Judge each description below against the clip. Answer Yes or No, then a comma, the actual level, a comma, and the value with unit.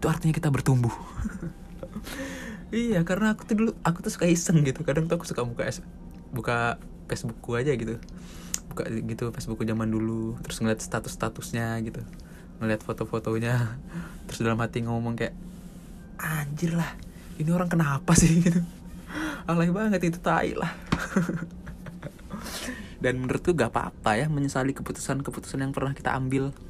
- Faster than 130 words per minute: Yes, fast, 140 wpm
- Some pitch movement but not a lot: No, wide, 6.7 semitones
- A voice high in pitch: No, medium, 145 Hz